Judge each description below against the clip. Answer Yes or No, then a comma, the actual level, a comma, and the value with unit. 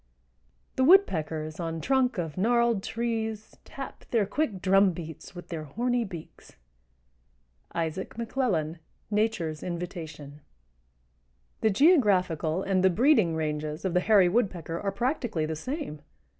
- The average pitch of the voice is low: No, high, 190 Hz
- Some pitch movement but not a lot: No, wide, 6.3 semitones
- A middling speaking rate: No, slow, 130 wpm